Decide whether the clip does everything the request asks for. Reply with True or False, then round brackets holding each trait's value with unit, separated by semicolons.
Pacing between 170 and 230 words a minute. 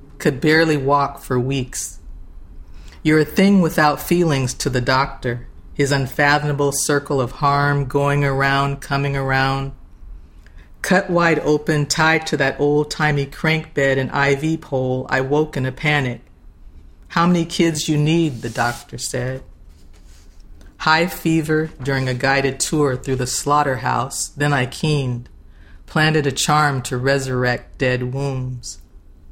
False (135 wpm)